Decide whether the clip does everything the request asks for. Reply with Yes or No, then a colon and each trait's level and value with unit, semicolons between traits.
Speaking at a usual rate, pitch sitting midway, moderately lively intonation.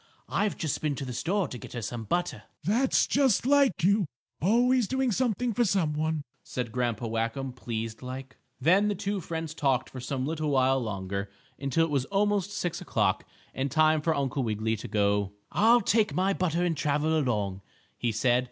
No: average, 190 wpm; medium, 150 Hz; wide, 8.0 semitones